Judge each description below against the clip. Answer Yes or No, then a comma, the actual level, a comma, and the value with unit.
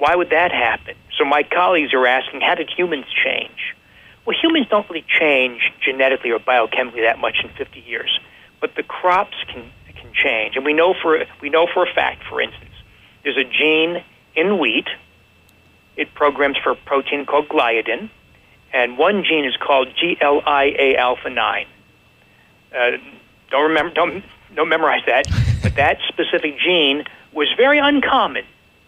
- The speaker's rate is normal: Yes, average, 150 wpm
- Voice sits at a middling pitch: Yes, medium, 145 Hz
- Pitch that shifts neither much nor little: No, wide, 6.1 semitones